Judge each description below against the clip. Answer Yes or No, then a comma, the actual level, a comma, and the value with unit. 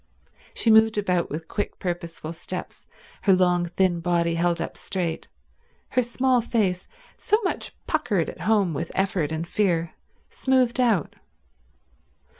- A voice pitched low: No, medium, 180 Hz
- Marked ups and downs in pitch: No, average, 4.6 semitones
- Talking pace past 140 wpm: No, slow, 135 wpm